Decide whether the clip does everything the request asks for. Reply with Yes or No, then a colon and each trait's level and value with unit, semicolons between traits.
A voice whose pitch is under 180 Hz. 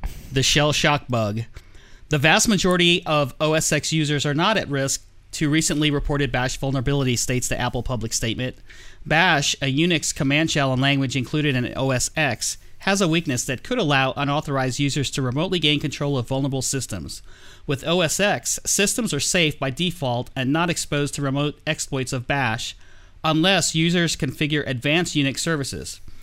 Yes: medium, 140 Hz